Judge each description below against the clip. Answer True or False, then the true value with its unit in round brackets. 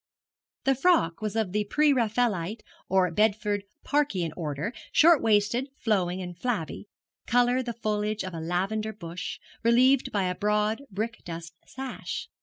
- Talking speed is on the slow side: False (145 wpm)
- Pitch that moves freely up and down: False (4.8 semitones)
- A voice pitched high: True (210 Hz)